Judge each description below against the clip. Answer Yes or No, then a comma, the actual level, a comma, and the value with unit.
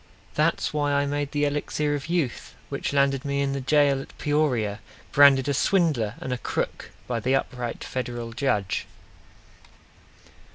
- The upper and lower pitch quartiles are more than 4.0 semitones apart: No, narrow, 2.6 semitones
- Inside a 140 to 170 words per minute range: Yes, average, 155 wpm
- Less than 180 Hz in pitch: Yes, medium, 140 Hz